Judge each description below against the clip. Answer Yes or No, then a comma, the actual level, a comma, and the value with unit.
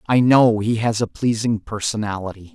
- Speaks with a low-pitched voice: Yes, low, 110 Hz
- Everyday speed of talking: Yes, average, 165 wpm